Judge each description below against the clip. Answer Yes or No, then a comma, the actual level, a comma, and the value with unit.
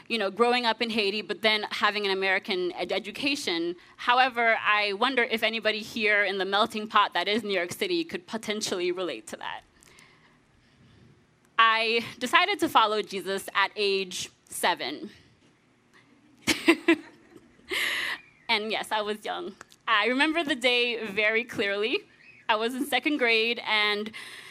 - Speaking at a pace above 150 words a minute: No, average, 140 wpm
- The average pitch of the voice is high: Yes, high, 215 Hz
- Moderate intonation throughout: Yes, average, 3.6 semitones